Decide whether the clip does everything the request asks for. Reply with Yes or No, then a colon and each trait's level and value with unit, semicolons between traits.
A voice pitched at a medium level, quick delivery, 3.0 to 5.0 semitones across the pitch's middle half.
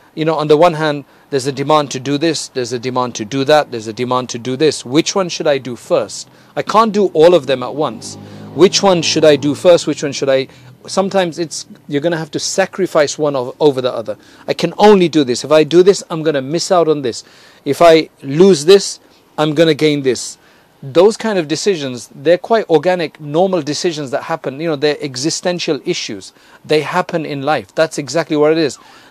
Yes: medium, 155 Hz; fast, 225 wpm; average, 3.6 semitones